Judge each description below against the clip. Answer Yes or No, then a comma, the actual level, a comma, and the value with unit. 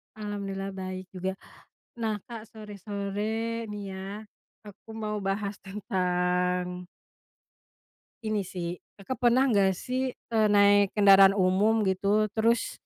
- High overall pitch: Yes, high, 200 Hz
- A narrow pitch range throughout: Yes, narrow, 2.3 semitones